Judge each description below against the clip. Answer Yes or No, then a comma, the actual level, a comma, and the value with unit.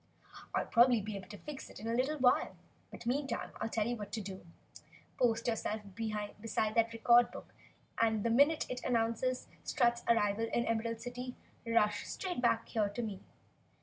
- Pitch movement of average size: No, narrow, 2.2 semitones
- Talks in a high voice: Yes, high, 230 Hz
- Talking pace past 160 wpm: Yes, average, 185 wpm